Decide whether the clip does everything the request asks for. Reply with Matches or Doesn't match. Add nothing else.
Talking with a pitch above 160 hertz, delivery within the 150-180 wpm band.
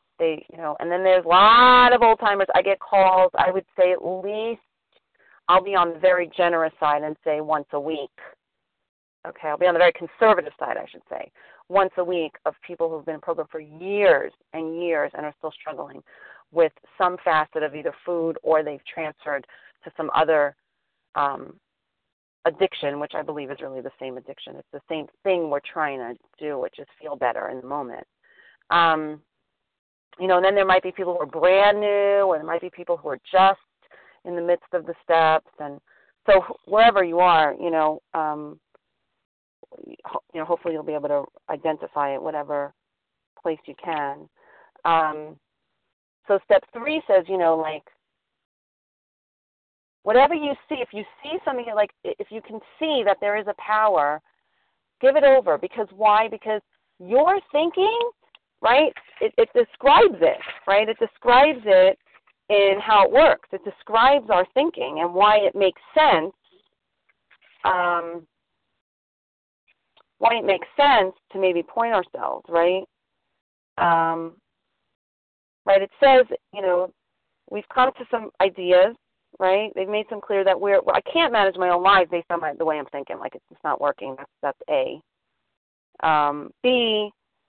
Matches